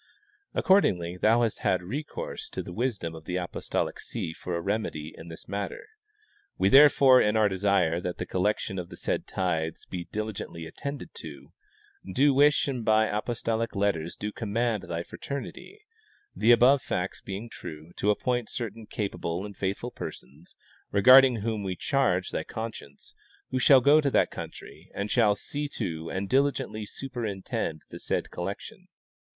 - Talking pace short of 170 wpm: Yes, average, 160 wpm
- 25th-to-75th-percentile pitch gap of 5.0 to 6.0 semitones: Yes, wide, 5.5 semitones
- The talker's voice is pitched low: Yes, low, 105 Hz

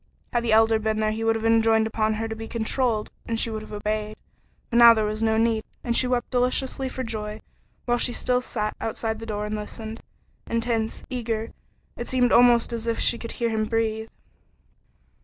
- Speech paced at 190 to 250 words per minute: Yes, fast, 205 wpm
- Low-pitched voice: No, high, 225 Hz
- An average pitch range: No, narrow, 1.4 semitones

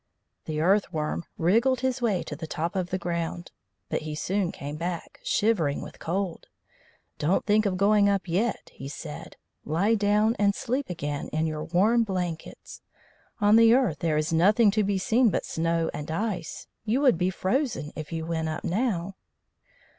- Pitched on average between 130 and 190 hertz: Yes, medium, 185 Hz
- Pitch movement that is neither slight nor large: Yes, average, 4.7 semitones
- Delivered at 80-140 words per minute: No, average, 175 wpm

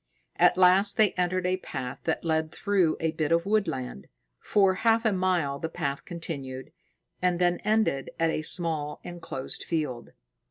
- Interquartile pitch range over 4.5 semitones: No, average, 3.5 semitones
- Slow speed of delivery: No, average, 160 wpm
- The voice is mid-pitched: Yes, medium, 170 Hz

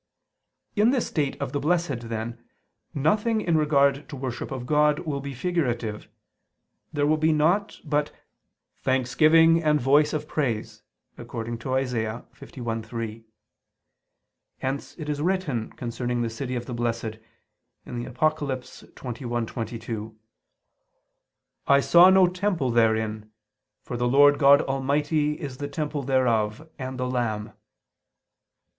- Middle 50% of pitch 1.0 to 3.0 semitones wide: No, average, 4.2 semitones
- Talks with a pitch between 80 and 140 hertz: Yes, low, 135 Hz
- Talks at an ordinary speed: No, slow, 120 wpm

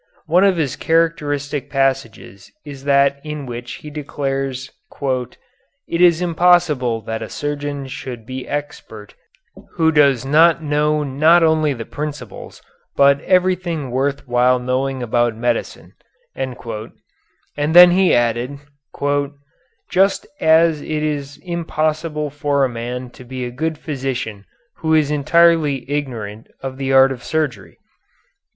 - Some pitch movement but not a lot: Yes, average, 3.5 semitones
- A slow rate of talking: Yes, slow, 130 wpm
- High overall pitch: No, medium, 140 Hz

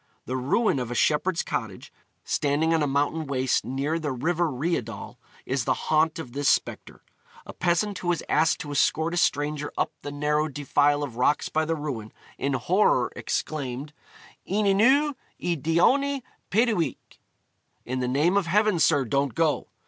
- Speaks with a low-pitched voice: No, medium, 150 Hz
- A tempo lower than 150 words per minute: No, average, 165 wpm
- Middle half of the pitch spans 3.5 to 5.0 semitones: Yes, average, 3.8 semitones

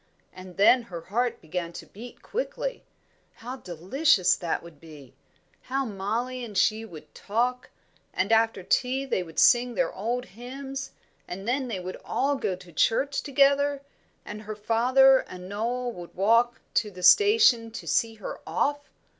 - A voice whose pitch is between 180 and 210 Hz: No, high, 230 Hz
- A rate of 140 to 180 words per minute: Yes, average, 160 wpm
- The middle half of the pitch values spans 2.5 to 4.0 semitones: No, wide, 5.5 semitones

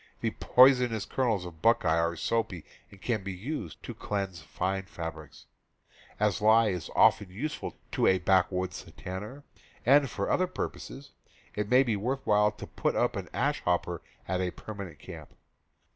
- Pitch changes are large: No, average, 4.2 semitones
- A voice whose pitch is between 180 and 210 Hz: No, low, 100 Hz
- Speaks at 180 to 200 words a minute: No, average, 165 wpm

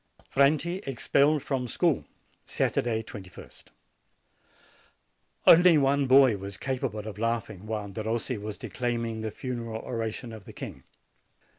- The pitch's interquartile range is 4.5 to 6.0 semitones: No, average, 3.7 semitones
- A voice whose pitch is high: No, low, 115 Hz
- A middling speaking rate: No, slow, 120 wpm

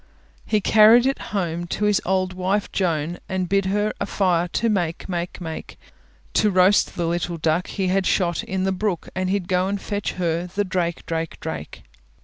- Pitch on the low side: No, medium, 185 Hz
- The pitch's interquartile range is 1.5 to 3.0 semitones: Yes, narrow, 2.6 semitones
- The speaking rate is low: No, average, 195 wpm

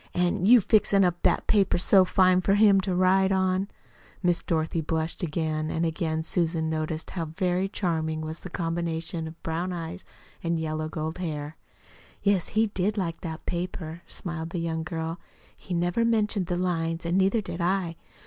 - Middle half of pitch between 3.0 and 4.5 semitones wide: No, narrow, 2.6 semitones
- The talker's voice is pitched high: No, medium, 175 Hz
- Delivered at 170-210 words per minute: Yes, average, 175 wpm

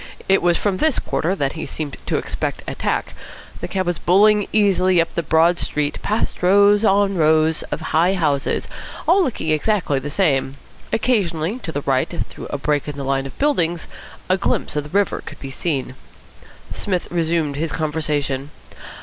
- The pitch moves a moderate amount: Yes, average, 4.8 semitones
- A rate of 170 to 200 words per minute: Yes, average, 175 wpm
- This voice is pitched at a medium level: Yes, medium, 165 Hz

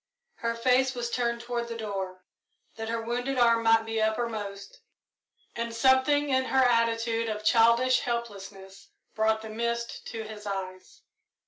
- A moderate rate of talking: Yes, average, 145 wpm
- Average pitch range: No, narrow, 1.7 semitones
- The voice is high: Yes, high, 230 Hz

